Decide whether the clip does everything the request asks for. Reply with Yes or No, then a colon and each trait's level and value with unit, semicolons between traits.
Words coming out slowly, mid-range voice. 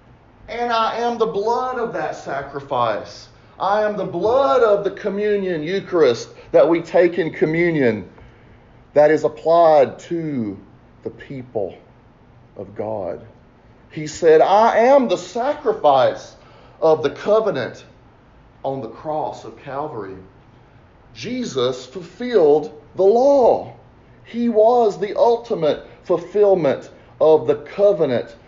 Yes: slow, 115 wpm; medium, 175 Hz